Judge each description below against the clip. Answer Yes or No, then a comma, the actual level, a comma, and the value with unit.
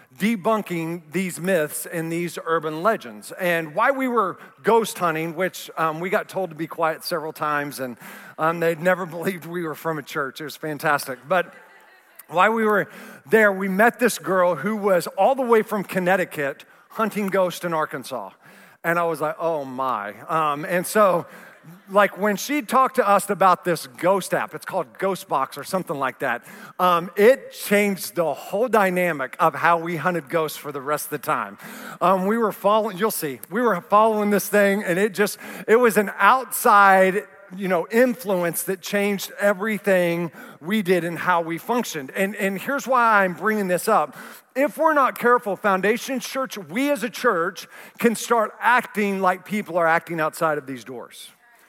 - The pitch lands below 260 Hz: Yes, high, 190 Hz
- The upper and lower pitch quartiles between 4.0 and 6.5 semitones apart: Yes, average, 4.3 semitones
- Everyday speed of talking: Yes, average, 185 wpm